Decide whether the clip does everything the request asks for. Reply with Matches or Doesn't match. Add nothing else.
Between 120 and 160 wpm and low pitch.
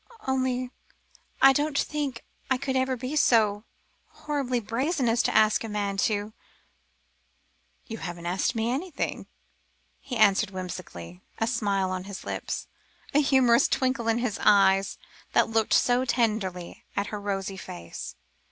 Doesn't match